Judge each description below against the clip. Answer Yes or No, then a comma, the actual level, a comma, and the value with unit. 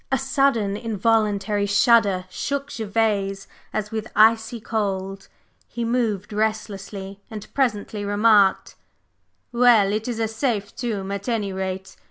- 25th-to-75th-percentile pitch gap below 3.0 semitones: Yes, narrow, 2.4 semitones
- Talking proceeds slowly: Yes, slow, 125 wpm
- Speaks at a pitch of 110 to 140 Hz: No, high, 215 Hz